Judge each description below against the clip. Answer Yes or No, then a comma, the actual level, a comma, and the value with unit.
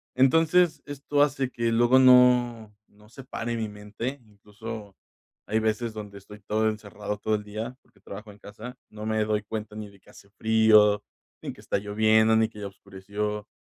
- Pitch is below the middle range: Yes, low, 110 Hz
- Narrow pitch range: Yes, narrow, 2.3 semitones